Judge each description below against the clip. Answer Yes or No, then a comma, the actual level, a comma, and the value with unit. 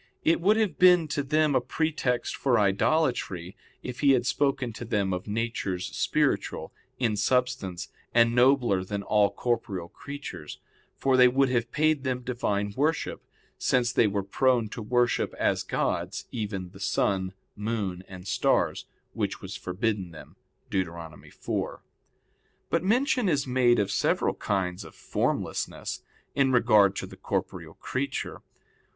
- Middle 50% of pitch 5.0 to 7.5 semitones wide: Yes, wide, 5.4 semitones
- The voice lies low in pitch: Yes, low, 120 Hz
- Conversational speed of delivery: Yes, average, 145 wpm